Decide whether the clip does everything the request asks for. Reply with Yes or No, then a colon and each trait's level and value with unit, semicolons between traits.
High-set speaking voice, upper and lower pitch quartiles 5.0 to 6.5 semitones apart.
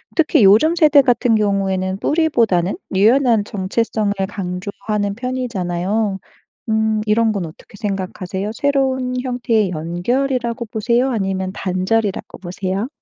No: high, 215 Hz; average, 4.3 semitones